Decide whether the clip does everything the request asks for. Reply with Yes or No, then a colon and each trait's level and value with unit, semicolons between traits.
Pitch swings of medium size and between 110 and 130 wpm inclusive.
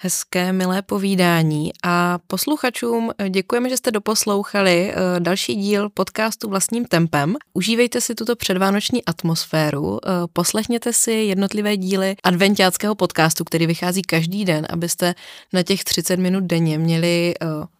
Yes: average, 3.2 semitones; average, 120 wpm